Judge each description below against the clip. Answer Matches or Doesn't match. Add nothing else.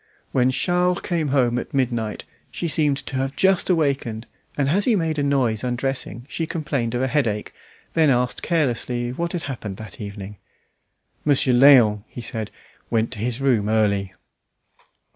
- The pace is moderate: Matches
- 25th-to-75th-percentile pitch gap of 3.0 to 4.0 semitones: Doesn't match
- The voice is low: Matches